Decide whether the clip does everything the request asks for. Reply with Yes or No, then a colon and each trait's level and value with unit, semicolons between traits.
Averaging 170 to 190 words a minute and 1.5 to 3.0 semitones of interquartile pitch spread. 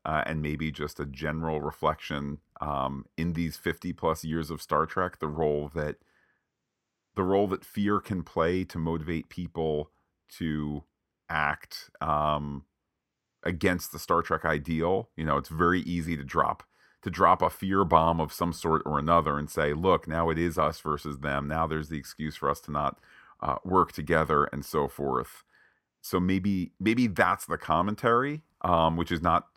Yes: average, 175 wpm; narrow, 2.6 semitones